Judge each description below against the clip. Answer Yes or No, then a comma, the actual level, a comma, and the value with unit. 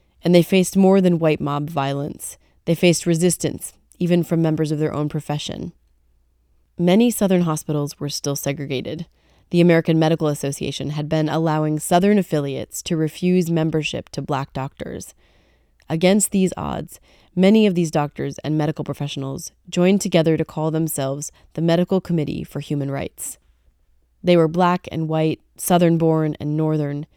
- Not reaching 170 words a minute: Yes, average, 150 wpm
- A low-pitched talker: No, medium, 155 Hz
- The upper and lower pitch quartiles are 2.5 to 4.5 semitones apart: Yes, average, 3.3 semitones